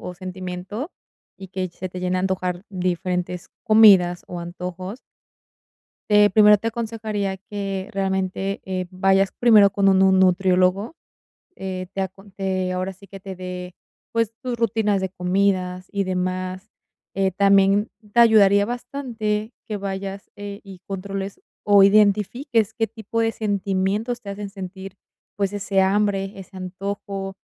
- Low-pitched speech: No, high, 195 Hz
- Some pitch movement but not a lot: No, narrow, 1.9 semitones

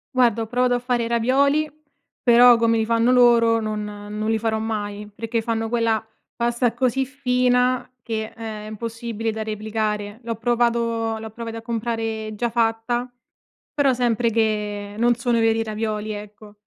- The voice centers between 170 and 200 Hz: No, high, 230 Hz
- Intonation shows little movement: Yes, narrow, 1.7 semitones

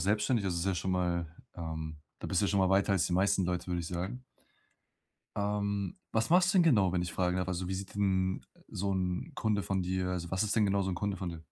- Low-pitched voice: Yes, very low, 95 Hz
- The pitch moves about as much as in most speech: No, narrow, 2.3 semitones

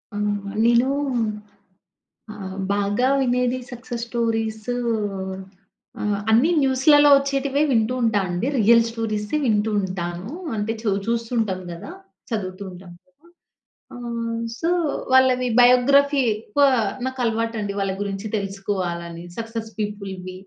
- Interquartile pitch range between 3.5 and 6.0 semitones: Yes, average, 3.8 semitones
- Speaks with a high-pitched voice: Yes, high, 225 Hz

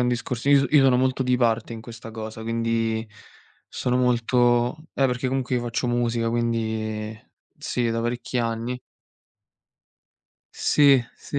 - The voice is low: Yes, low, 120 Hz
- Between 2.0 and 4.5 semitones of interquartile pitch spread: No, narrow, 1.6 semitones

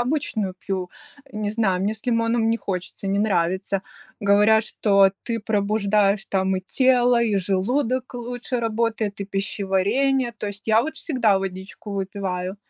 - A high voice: Yes, high, 210 Hz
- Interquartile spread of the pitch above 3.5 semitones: No, average, 3.1 semitones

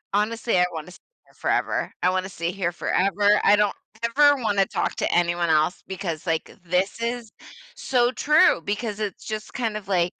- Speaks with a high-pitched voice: Yes, high, 200 Hz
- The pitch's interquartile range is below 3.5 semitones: No, average, 4.0 semitones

